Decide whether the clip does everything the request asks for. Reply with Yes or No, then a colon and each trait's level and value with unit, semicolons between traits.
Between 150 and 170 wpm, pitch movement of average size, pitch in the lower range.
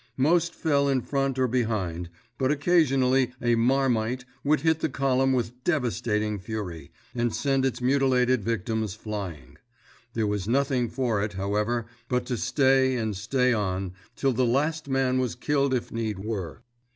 Yes: average, 155 wpm; average, 3.9 semitones; low, 125 Hz